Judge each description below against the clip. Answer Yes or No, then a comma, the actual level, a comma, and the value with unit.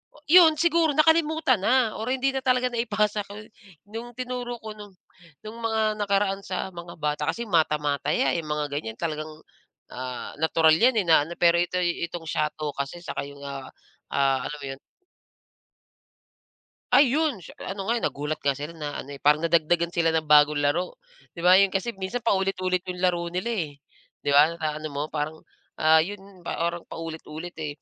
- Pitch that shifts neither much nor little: No, wide, 6.0 semitones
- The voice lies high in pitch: No, medium, 175 Hz